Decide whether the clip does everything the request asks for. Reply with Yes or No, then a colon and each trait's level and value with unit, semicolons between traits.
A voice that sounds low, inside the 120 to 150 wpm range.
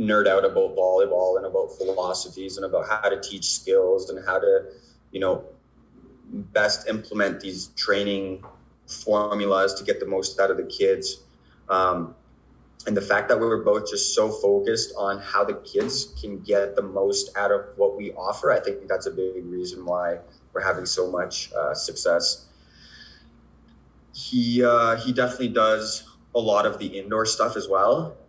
No: low, 125 Hz; average, 170 wpm